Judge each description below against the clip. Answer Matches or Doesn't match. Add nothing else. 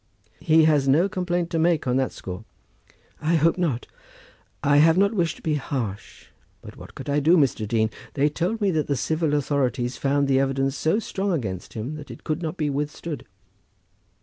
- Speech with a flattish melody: Doesn't match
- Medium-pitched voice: Matches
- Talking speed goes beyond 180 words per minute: Matches